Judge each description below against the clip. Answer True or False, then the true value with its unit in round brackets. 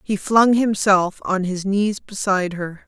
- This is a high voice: True (195 Hz)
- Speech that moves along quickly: False (165 wpm)